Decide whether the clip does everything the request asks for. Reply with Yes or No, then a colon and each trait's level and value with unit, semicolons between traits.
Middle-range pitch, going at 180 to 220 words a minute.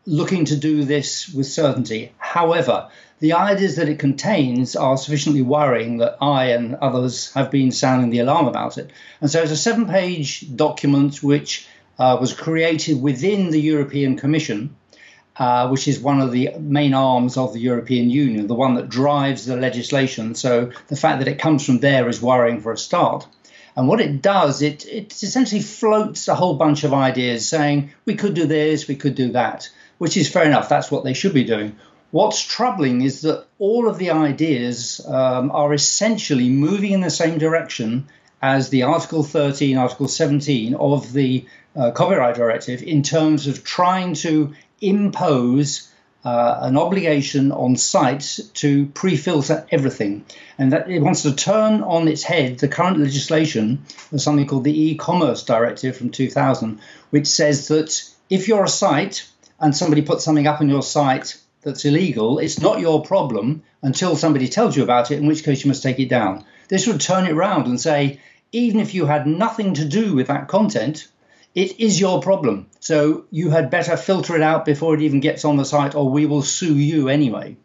Yes: medium, 145 Hz; average, 185 wpm